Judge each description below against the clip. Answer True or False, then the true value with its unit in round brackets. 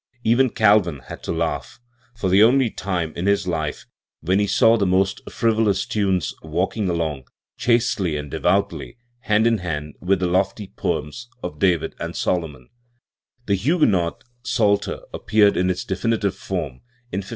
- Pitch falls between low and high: False (95 Hz)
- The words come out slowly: False (155 wpm)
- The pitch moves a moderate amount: True (4.1 semitones)